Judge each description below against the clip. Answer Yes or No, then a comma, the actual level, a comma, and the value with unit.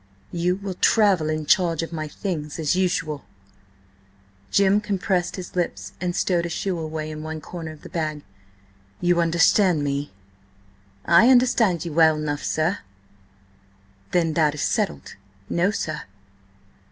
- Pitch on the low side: No, medium, 170 Hz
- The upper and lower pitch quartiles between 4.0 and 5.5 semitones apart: No, average, 2.9 semitones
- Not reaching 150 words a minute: Yes, average, 140 wpm